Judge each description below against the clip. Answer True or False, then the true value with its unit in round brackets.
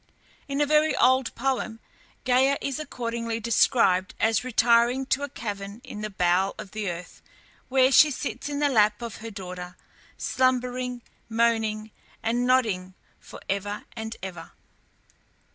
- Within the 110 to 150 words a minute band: True (145 wpm)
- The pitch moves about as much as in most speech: True (3.7 semitones)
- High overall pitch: True (230 Hz)